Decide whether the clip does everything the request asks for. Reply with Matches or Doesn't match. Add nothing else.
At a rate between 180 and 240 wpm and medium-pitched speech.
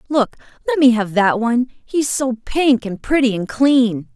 Doesn't match